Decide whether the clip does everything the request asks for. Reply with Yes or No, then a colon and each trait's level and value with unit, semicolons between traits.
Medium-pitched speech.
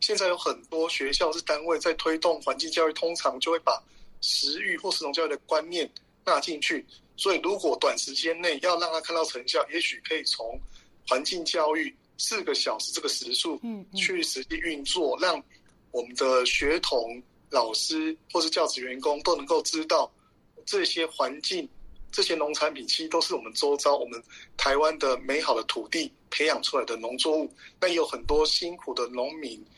Yes: medium, 175 Hz